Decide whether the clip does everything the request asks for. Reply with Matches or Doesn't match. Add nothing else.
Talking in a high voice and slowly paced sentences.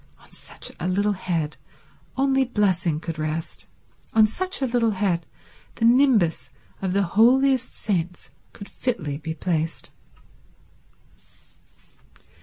Matches